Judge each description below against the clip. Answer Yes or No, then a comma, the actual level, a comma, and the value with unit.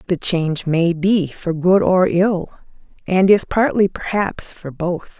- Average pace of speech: Yes, average, 160 wpm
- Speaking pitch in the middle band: Yes, medium, 180 Hz